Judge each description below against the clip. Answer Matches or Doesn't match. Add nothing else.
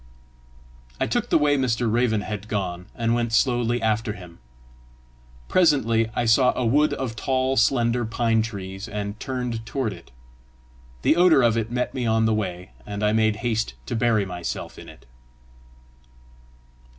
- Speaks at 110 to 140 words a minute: Doesn't match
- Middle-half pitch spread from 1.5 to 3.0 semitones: Matches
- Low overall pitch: Matches